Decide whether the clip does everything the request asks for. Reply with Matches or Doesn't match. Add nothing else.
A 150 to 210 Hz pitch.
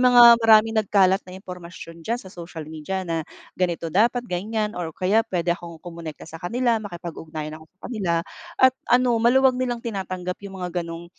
Matches